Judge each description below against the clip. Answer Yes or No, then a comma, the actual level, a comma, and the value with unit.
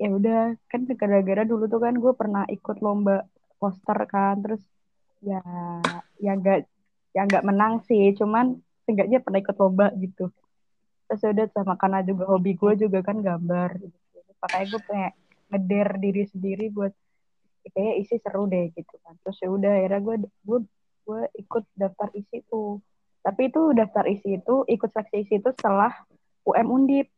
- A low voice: No, high, 200 Hz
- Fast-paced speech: Yes, fast, 160 wpm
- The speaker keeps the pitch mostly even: Yes, narrow, 2.3 semitones